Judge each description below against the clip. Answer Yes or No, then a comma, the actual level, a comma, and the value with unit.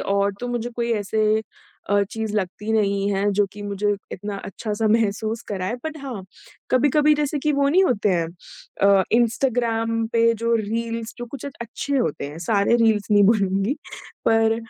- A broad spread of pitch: No, average, 2.8 semitones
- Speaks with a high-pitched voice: Yes, high, 225 Hz